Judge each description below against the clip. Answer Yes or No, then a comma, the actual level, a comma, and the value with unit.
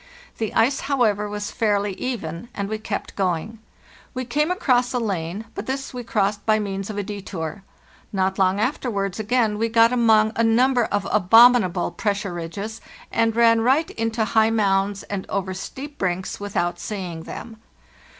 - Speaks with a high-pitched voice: Yes, high, 215 Hz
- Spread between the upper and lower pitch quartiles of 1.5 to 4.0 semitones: Yes, average, 2.9 semitones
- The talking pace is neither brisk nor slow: Yes, average, 165 wpm